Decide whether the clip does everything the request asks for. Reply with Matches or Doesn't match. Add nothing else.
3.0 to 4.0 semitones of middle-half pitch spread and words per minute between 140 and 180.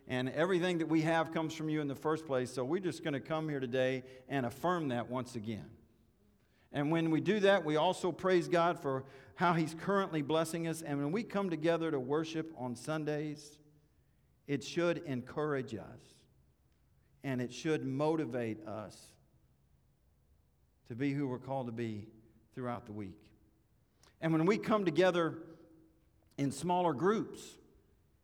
Doesn't match